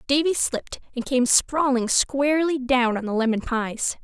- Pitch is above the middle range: Yes, very high, 260 Hz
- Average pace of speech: Yes, average, 165 wpm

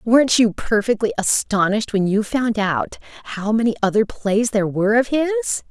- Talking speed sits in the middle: Yes, average, 170 wpm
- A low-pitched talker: No, high, 215 Hz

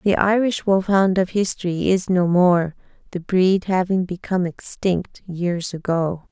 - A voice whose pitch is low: No, medium, 185 Hz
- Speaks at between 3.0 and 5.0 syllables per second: Yes, 4.2 syllables/s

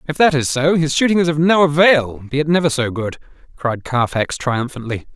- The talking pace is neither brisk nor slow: No, fast, 210 wpm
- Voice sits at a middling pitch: Yes, medium, 145 Hz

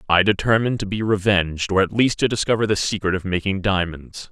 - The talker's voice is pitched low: Yes, low, 100 Hz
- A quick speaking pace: Yes, fast, 210 wpm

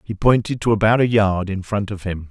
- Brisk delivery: Yes, fast, 260 wpm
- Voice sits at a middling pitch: No, low, 105 Hz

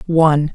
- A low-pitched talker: No, medium, 155 Hz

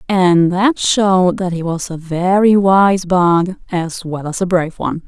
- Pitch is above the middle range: No, medium, 180 Hz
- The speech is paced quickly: No, average, 190 wpm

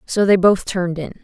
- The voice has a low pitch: No, medium, 185 Hz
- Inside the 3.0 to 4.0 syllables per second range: No, 5.8 syllables/s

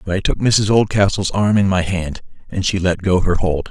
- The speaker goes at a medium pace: No, fast, 245 wpm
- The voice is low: Yes, very low, 95 Hz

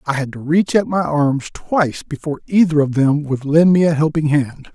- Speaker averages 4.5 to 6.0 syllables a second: Yes, 5.2 syllables/s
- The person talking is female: No, male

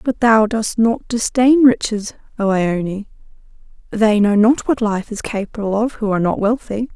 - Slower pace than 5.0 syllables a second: Yes, 4.5 syllables/s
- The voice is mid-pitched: No, high, 220 Hz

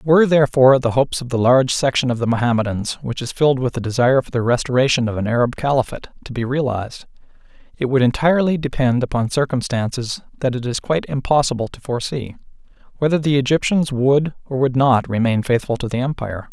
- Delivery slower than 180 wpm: No, average, 185 wpm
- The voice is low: Yes, low, 130 Hz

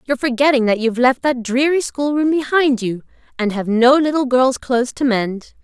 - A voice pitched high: Yes, very high, 255 Hz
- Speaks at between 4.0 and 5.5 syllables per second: Yes, 5.4 syllables/s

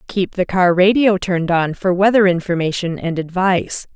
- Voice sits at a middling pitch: Yes, medium, 180 Hz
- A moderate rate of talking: Yes, average, 165 wpm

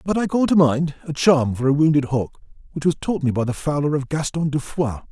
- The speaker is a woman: No, male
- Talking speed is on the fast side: Yes, fast, 260 wpm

